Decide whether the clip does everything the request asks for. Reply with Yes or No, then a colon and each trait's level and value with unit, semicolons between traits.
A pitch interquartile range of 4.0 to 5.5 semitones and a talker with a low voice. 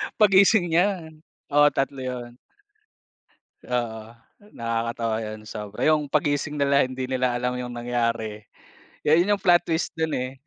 Yes: average, 4.9 semitones; low, 130 Hz